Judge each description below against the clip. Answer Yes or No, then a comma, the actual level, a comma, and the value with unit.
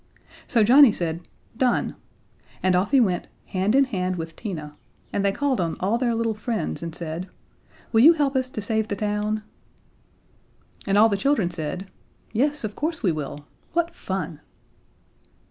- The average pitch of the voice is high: Yes, high, 210 Hz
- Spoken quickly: No, average, 165 wpm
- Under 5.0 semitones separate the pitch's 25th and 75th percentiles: No, wide, 5.6 semitones